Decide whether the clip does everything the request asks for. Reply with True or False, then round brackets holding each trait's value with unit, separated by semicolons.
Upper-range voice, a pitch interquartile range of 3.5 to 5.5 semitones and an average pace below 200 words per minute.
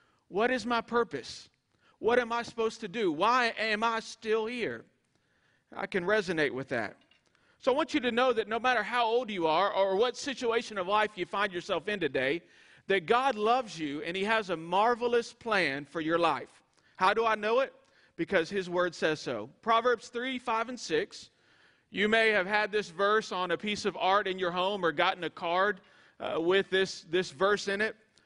False (210 Hz; 3.9 semitones; 205 wpm)